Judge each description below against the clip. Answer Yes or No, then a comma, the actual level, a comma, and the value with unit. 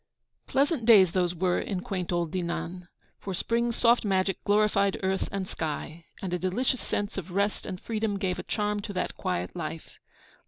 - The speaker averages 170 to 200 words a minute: Yes, average, 180 wpm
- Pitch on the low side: No, high, 195 Hz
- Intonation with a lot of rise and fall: No, average, 2.8 semitones